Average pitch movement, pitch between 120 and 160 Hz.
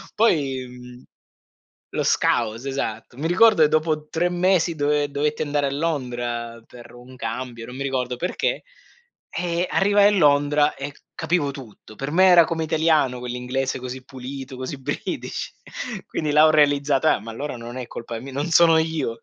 Yes: average, 4.1 semitones; medium, 140 Hz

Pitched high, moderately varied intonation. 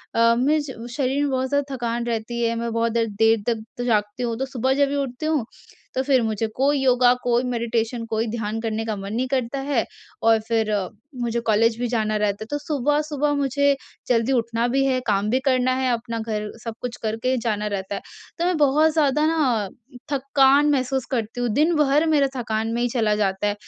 Yes: high, 240 Hz; average, 3.3 semitones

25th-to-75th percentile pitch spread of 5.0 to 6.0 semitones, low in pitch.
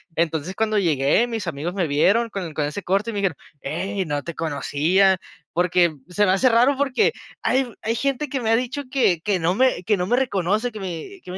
No: wide, 5.5 semitones; high, 195 Hz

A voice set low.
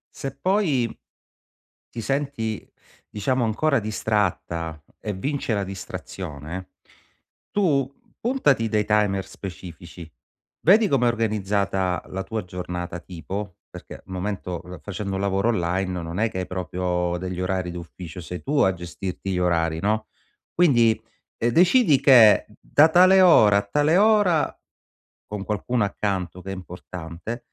Yes: low, 100 Hz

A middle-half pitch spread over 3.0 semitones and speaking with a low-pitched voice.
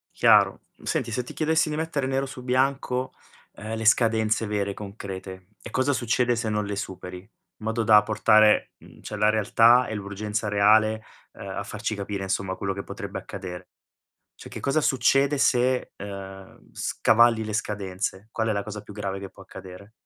Yes: average, 3.4 semitones; low, 110 Hz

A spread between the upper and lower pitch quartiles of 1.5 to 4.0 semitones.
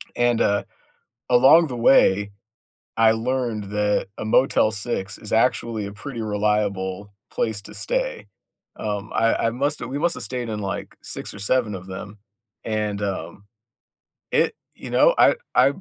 Yes: average, 3.4 semitones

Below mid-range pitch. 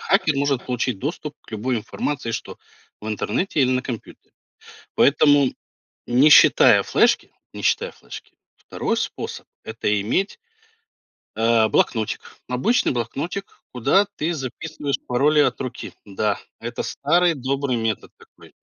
Yes: low, 130 Hz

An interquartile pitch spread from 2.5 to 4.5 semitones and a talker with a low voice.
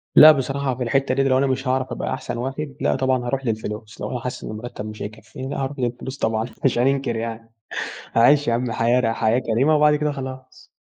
Yes: average, 2.9 semitones; low, 130 Hz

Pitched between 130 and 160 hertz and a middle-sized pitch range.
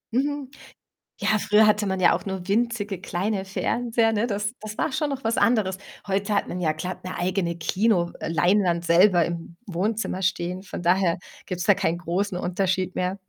No: high, 190 Hz; average, 3.3 semitones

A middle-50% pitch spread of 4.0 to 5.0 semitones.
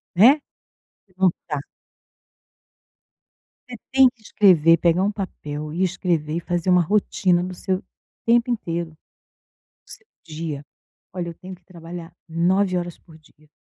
No: narrow, 2.5 semitones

